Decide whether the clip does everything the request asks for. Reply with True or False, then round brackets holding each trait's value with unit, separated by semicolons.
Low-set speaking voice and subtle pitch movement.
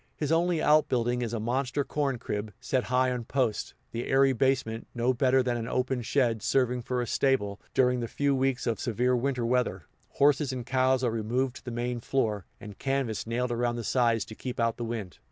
True (125 Hz; 2.3 semitones)